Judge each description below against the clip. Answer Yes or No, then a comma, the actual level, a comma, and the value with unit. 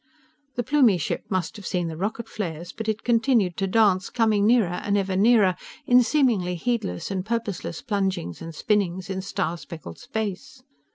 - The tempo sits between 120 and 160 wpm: No, average, 170 wpm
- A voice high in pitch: Yes, high, 200 Hz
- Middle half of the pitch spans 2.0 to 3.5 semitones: No, average, 3.9 semitones